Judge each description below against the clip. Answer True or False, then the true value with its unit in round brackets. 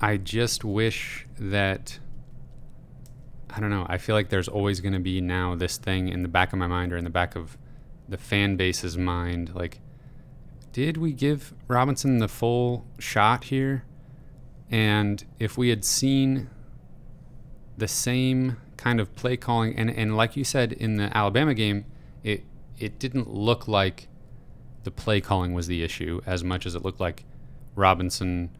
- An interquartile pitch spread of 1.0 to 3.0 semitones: False (5.4 semitones)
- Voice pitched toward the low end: True (115 Hz)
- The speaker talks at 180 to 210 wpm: False (170 wpm)